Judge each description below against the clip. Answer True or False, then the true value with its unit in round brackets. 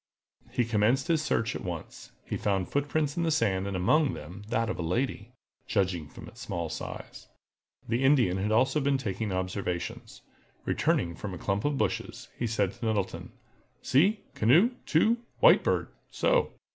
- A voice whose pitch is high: False (115 Hz)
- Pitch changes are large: True (6.9 semitones)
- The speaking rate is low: False (155 wpm)